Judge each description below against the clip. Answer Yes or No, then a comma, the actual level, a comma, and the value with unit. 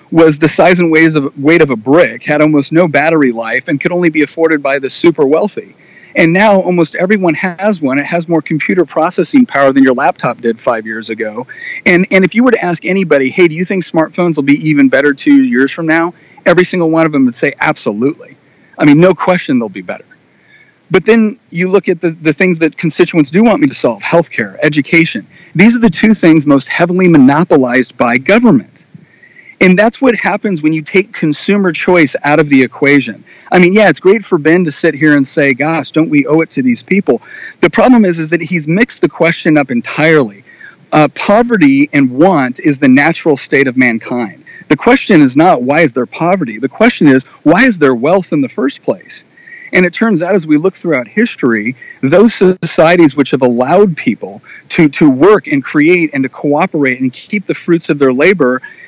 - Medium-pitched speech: Yes, medium, 170 Hz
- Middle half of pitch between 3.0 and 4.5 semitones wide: No, average, 5.2 semitones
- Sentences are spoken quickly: Yes, fast, 210 wpm